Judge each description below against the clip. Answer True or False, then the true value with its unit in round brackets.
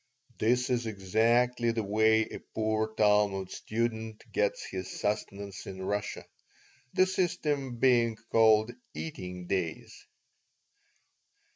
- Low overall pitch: True (110 Hz)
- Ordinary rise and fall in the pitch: True (3.0 semitones)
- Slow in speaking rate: True (105 wpm)